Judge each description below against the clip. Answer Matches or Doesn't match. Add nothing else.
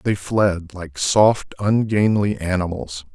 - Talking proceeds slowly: Matches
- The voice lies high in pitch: Doesn't match